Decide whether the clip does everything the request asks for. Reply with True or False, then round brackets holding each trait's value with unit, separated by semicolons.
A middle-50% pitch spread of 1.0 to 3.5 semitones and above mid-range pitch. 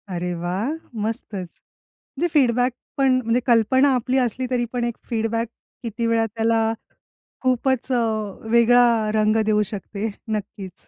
True (2.5 semitones; 230 Hz)